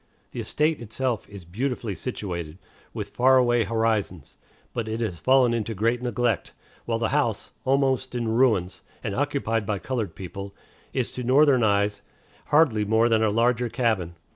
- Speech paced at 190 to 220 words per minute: No, average, 160 wpm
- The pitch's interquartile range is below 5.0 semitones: Yes, average, 3.7 semitones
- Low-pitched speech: Yes, low, 115 Hz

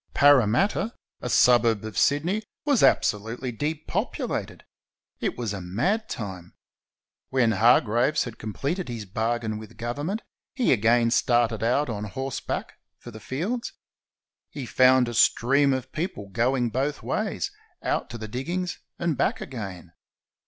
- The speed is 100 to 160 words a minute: Yes, average, 140 wpm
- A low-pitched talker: Yes, low, 120 Hz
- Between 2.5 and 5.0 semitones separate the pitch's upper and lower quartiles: Yes, average, 4.4 semitones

